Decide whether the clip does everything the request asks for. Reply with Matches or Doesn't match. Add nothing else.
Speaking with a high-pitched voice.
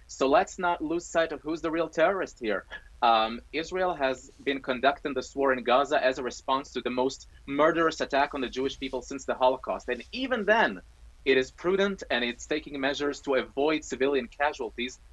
Doesn't match